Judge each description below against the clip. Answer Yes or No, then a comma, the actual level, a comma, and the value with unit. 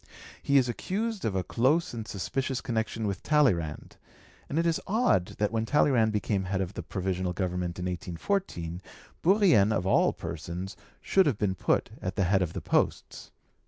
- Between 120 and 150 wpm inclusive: No, average, 175 wpm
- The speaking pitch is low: Yes, low, 105 Hz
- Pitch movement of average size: No, wide, 7.2 semitones